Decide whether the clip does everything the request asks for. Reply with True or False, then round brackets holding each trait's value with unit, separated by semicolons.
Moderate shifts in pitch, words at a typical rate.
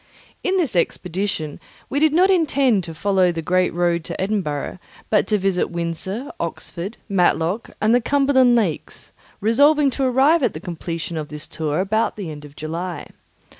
False (6.8 semitones; 170 wpm)